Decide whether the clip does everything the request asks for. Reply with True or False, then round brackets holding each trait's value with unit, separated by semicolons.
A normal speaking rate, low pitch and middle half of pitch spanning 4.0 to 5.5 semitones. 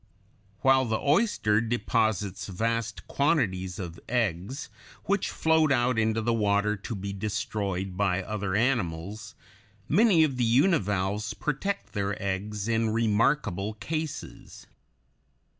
False (120 wpm; 110 Hz; 4.3 semitones)